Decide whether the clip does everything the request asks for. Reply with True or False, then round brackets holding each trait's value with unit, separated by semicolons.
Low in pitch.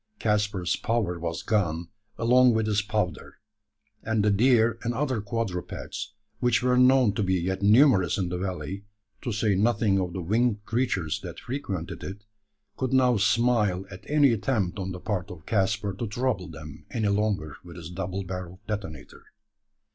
True (105 Hz)